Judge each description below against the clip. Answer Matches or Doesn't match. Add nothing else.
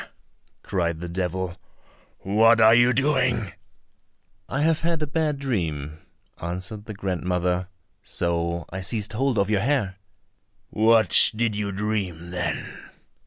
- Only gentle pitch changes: Doesn't match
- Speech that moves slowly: Matches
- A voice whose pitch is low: Matches